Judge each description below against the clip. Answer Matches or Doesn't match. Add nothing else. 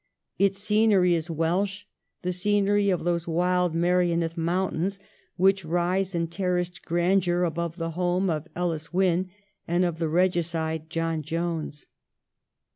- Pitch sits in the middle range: Matches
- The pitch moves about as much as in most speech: Doesn't match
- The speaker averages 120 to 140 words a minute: Matches